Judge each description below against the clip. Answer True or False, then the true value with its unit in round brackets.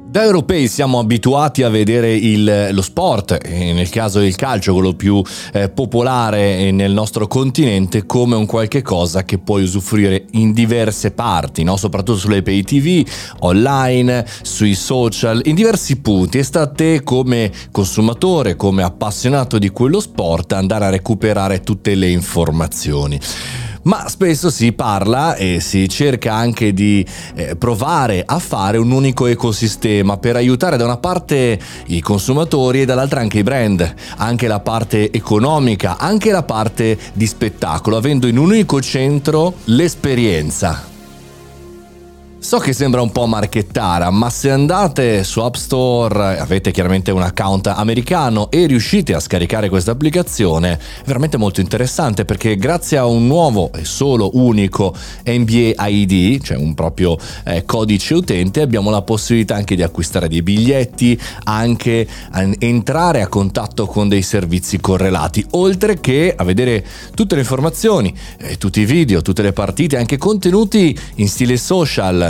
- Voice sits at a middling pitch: False (110 Hz)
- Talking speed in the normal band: True (150 wpm)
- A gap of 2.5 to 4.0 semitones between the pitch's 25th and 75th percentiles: False (5.0 semitones)